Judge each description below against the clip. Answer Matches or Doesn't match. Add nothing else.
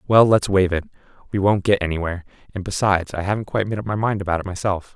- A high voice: Doesn't match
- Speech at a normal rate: Doesn't match